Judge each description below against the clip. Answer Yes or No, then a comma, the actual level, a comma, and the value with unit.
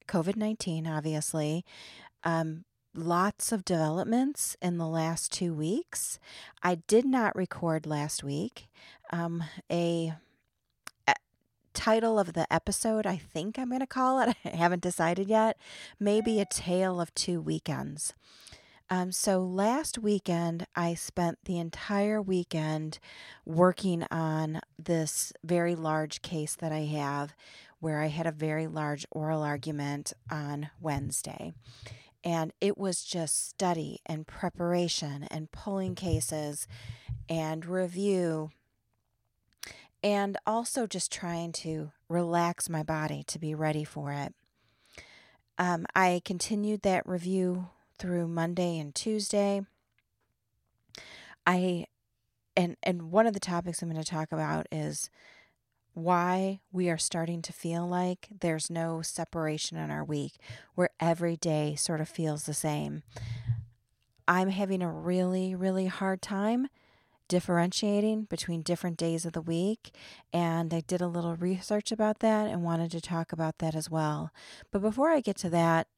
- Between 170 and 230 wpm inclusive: No, slow, 135 wpm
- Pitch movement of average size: Yes, average, 3.1 semitones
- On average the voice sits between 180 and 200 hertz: No, medium, 170 Hz